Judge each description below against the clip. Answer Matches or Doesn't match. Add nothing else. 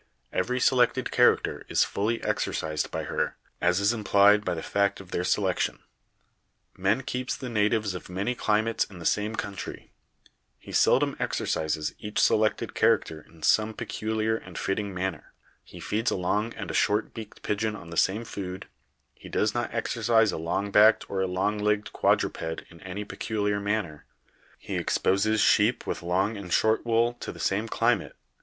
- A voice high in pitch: Doesn't match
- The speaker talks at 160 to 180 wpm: Matches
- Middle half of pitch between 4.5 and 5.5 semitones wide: Doesn't match